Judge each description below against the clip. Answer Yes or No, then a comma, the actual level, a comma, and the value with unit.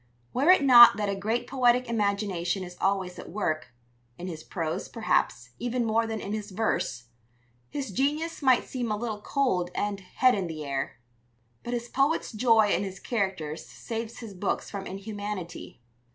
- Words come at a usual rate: Yes, average, 170 wpm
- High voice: Yes, high, 210 Hz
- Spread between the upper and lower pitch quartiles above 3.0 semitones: Yes, average, 4.3 semitones